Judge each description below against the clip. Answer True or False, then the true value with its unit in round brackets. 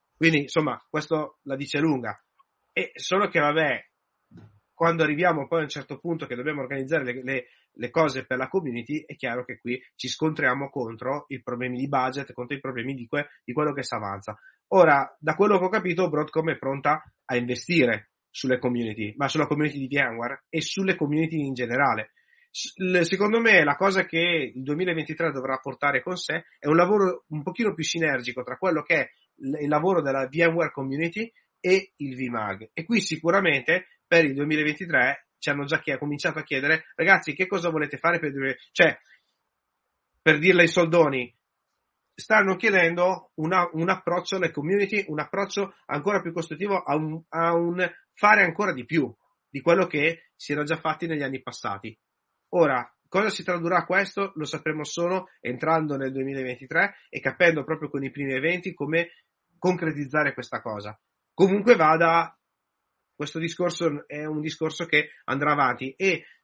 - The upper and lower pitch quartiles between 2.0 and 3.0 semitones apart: False (4.3 semitones)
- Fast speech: True (175 wpm)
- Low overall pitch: False (155 Hz)